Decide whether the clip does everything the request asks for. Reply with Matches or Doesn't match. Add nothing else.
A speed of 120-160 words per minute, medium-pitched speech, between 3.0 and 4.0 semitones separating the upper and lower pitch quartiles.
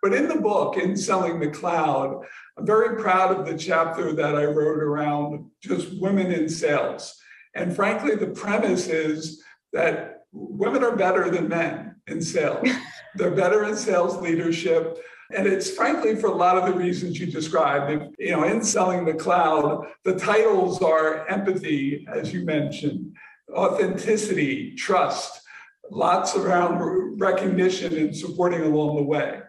Matches